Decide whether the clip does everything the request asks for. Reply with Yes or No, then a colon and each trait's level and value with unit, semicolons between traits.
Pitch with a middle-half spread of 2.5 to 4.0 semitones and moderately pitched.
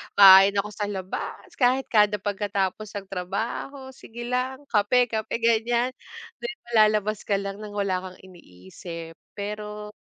No: average, 3.0 semitones; high, 210 Hz